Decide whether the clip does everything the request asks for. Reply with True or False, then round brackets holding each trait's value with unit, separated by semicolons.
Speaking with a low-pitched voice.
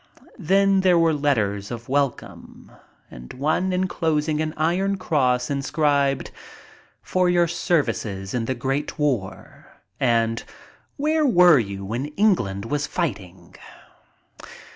False (145 Hz)